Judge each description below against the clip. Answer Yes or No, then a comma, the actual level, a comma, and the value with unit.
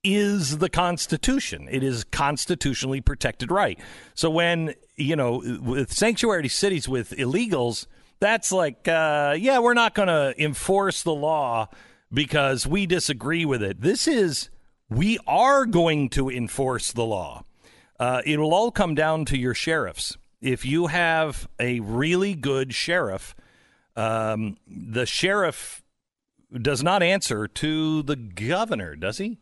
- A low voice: No, medium, 150 Hz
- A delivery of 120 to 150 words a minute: Yes, average, 140 wpm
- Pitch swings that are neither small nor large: No, wide, 6.2 semitones